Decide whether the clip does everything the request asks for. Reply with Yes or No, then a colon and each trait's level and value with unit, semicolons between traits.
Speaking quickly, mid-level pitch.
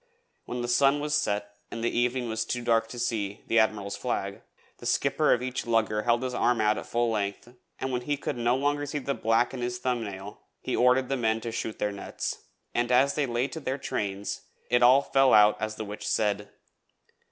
No: fast, 225 wpm; low, 120 Hz